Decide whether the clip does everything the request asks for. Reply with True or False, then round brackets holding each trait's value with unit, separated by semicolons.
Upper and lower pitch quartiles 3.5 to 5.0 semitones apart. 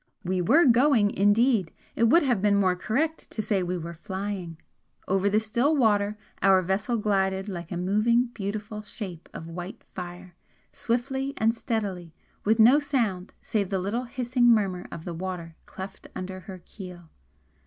True (4.0 semitones)